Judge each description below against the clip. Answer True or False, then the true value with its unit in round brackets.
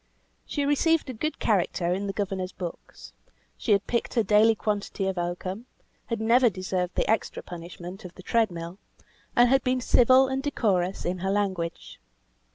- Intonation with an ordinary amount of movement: True (4.6 semitones)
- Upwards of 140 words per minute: True (170 wpm)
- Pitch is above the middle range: True (200 Hz)